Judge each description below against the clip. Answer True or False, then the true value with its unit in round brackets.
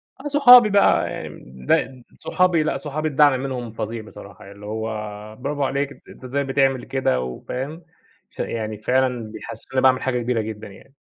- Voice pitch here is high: False (130 Hz)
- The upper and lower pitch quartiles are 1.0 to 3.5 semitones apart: False (4.3 semitones)